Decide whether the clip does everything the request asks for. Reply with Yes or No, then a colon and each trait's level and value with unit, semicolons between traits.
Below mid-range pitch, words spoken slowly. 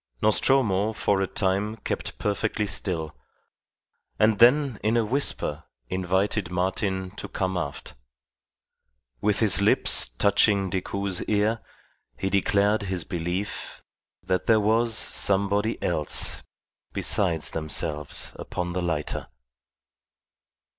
Yes: low, 100 Hz; slow, 105 wpm